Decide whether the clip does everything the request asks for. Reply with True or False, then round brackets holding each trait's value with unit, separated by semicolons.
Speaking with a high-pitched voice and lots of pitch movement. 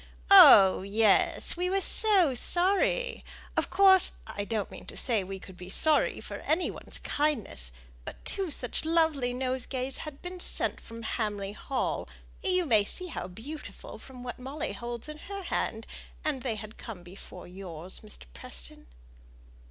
True (250 Hz; 8.2 semitones)